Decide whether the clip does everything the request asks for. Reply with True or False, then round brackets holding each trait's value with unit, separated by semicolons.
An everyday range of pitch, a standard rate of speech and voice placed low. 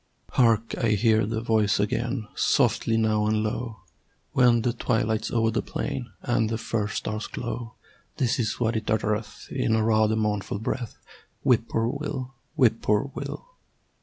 False (1.7 semitones; 160 wpm; 110 Hz)